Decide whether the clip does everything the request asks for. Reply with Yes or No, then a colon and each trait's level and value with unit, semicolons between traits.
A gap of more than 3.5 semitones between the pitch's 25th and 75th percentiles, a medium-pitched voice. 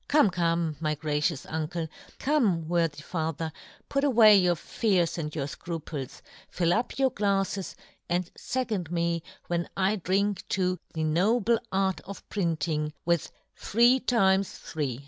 Yes: average, 4.1 semitones; medium, 175 Hz